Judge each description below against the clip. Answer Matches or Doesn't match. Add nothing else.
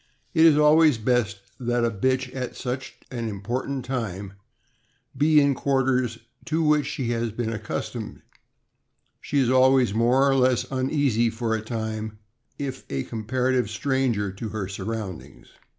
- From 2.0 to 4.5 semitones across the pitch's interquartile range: Matches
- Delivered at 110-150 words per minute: Matches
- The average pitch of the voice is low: Matches